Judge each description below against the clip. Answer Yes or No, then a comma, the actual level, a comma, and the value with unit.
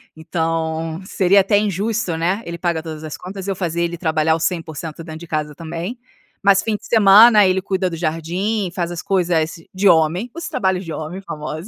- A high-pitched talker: No, medium, 175 Hz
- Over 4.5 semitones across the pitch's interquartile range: No, average, 3.3 semitones